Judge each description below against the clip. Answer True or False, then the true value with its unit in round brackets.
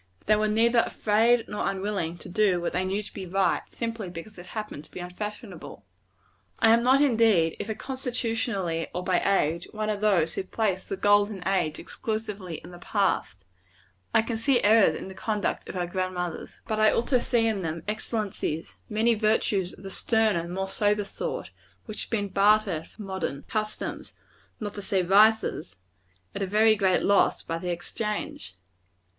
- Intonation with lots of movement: False (3.3 semitones)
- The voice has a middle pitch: False (205 Hz)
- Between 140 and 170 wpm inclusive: False (180 wpm)